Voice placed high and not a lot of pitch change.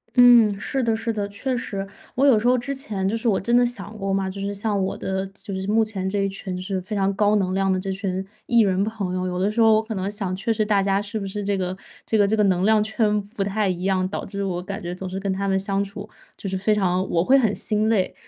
Yes: high, 200 Hz; narrow, 2.3 semitones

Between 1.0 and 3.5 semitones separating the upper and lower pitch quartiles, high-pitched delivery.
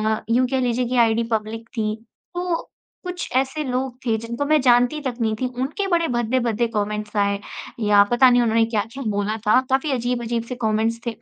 Yes: average, 2.8 semitones; high, 240 Hz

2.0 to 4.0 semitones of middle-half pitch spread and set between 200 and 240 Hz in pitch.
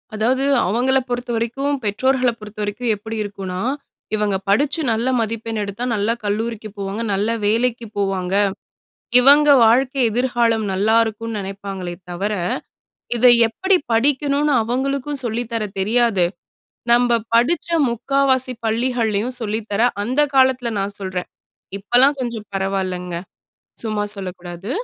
Yes: average, 3.6 semitones; high, 225 Hz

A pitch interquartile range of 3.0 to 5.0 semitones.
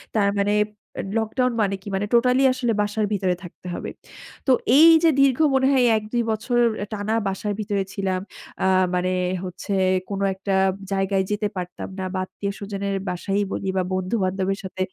No: narrow, 2.4 semitones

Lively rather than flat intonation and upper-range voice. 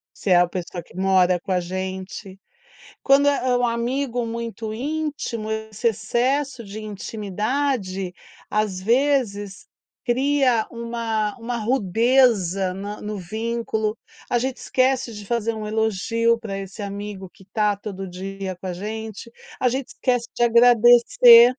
No: average, 3.5 semitones; high, 220 Hz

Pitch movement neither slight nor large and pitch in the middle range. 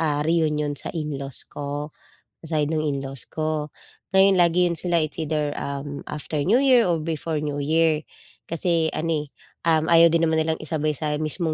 No: narrow, 1.9 semitones; medium, 155 Hz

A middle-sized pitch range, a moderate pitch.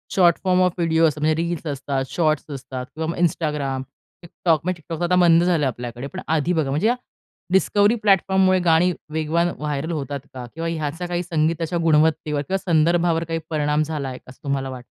Yes: average, 3.0 semitones; medium, 160 Hz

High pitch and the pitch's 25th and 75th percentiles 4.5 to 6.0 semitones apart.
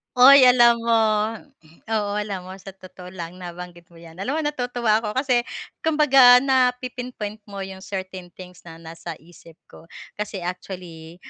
Yes: high, 195 Hz; wide, 5.6 semitones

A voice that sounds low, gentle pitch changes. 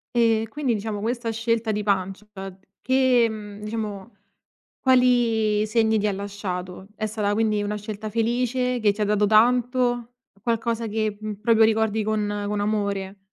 No: high, 215 Hz; narrow, 2.0 semitones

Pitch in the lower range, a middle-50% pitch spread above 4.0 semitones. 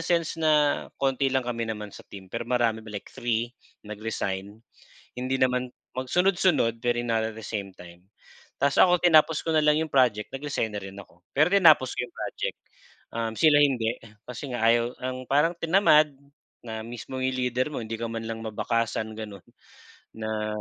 Yes: low, 120 Hz; average, 4.6 semitones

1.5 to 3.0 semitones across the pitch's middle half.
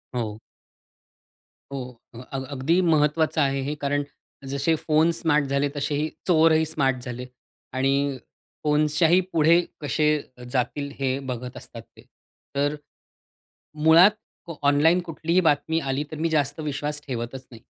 Yes: average, 2.7 semitones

